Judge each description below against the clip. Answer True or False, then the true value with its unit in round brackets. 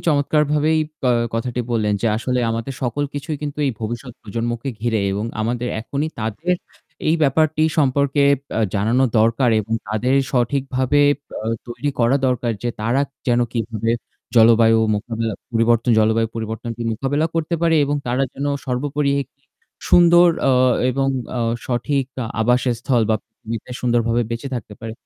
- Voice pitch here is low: True (120 Hz)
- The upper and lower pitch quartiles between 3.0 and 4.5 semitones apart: True (3.5 semitones)